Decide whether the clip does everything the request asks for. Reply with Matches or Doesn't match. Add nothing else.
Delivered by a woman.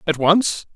Doesn't match